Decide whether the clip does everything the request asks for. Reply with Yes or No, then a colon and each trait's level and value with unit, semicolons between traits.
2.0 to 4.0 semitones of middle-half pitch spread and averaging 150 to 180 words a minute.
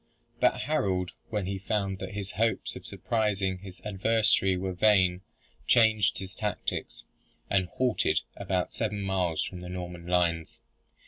No: narrow, 2.5 semitones; average, 140 wpm